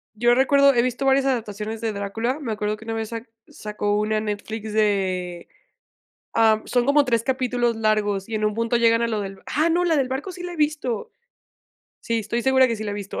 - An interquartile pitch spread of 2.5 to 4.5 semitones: Yes, average, 3.5 semitones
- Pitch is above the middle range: Yes, high, 230 Hz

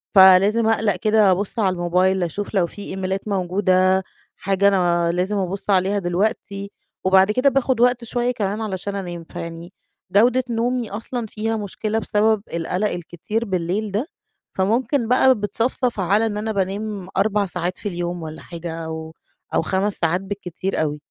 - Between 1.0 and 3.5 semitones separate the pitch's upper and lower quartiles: Yes, average, 3.2 semitones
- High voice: Yes, high, 195 Hz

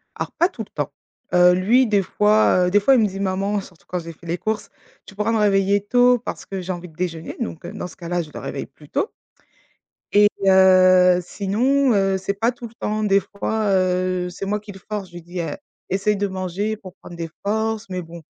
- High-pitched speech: Yes, high, 195 Hz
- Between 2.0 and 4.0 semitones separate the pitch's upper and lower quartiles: Yes, average, 2.8 semitones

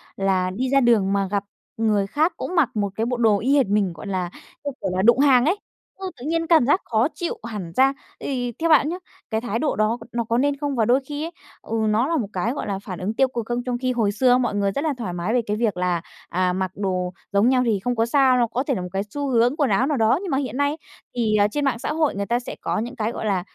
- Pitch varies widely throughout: No, average, 5.0 semitones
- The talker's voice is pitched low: No, high, 235 Hz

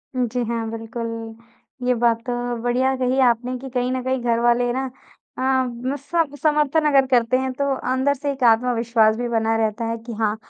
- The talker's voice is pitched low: No, high, 245 Hz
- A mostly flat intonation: Yes, narrow, 2.3 semitones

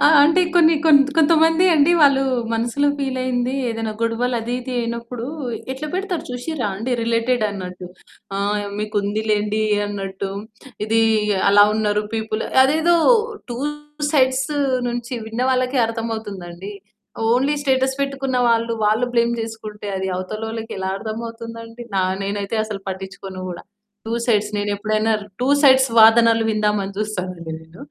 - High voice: Yes, high, 230 Hz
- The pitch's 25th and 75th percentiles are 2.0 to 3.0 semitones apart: No, average, 3.6 semitones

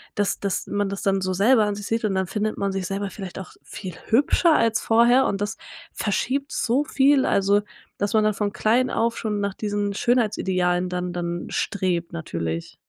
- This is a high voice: Yes, high, 205 Hz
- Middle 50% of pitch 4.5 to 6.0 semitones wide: No, average, 3.0 semitones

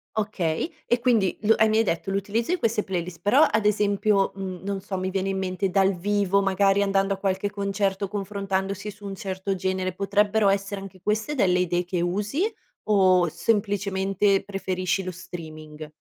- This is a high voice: Yes, high, 195 Hz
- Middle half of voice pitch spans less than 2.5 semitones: Yes, narrow, 1.7 semitones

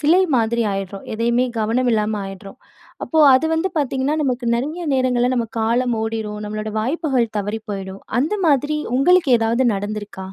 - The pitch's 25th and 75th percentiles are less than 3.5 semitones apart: No, average, 4.2 semitones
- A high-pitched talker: Yes, high, 235 Hz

